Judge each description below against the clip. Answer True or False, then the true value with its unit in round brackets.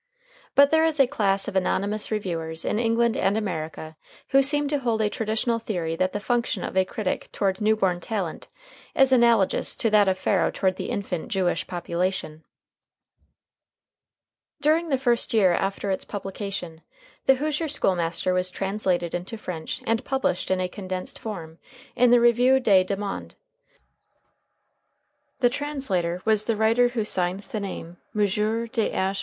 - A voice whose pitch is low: False (205 Hz)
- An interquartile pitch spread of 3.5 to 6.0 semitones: True (4.3 semitones)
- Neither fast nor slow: True (160 wpm)